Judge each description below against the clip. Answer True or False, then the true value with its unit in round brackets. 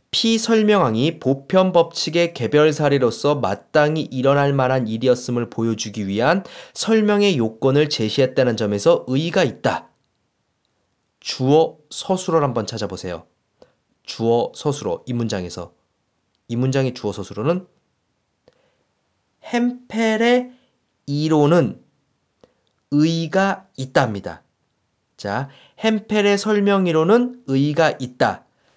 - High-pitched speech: False (145 Hz)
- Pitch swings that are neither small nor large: False (8.0 semitones)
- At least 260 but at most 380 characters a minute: False (240 characters per minute)